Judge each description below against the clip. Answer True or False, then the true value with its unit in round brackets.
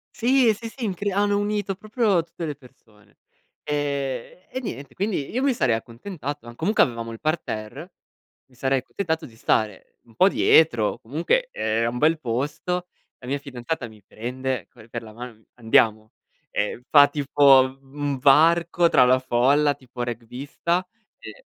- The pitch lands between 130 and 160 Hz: True (140 Hz)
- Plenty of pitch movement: True (6.5 semitones)